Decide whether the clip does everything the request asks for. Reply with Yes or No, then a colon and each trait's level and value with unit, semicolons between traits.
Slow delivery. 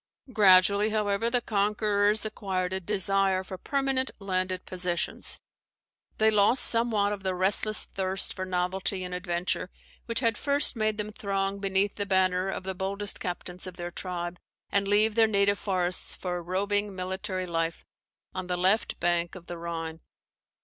No: average, 160 wpm